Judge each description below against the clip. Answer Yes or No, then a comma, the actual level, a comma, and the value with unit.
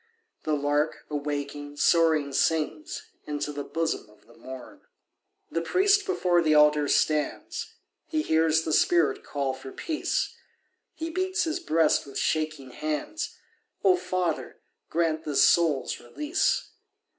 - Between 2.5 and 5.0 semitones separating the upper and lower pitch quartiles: Yes, average, 3.2 semitones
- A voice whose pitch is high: No, medium, 155 Hz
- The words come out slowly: Yes, slow, 130 wpm